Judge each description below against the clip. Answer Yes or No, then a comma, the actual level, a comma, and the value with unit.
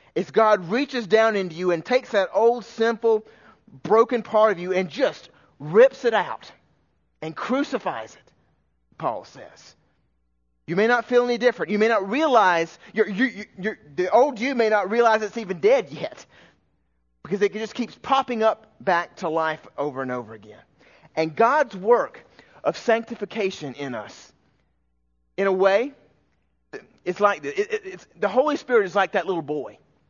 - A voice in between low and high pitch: No, high, 210 Hz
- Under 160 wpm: No, average, 170 wpm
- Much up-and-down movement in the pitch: Yes, wide, 6.1 semitones